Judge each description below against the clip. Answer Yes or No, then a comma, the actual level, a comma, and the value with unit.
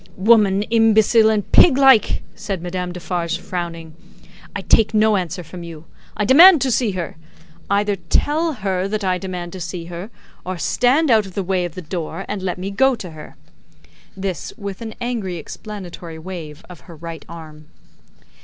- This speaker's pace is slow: No, average, 175 wpm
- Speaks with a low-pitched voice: No, high, 190 Hz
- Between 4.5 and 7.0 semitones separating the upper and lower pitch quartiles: No, average, 3.9 semitones